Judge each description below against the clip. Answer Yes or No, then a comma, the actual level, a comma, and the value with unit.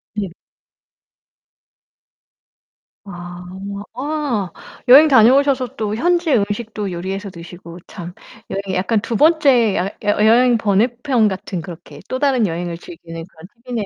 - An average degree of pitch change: No, wide, 5.8 semitones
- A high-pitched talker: Yes, high, 210 Hz